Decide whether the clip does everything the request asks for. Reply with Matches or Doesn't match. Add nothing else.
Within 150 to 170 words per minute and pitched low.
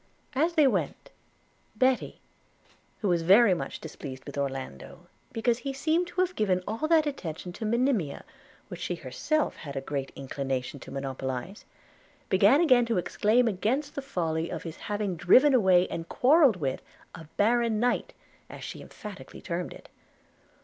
Doesn't match